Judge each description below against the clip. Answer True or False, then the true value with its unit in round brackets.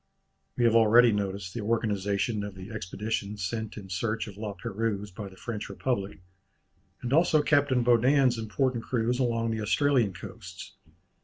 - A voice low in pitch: True (110 Hz)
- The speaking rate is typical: True (155 wpm)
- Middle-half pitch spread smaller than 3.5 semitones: True (3.0 semitones)